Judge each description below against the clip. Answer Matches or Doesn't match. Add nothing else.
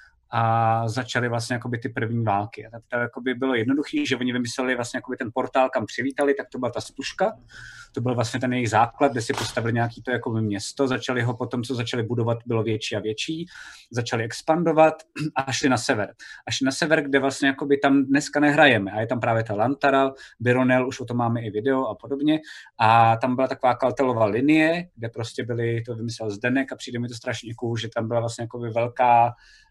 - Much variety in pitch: Doesn't match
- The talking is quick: Matches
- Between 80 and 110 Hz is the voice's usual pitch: Doesn't match